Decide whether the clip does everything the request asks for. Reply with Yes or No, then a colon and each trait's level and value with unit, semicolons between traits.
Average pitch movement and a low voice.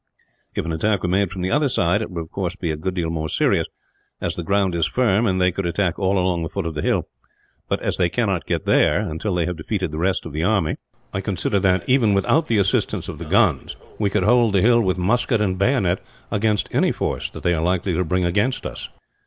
Yes: average, 3.3 semitones; very low, 95 Hz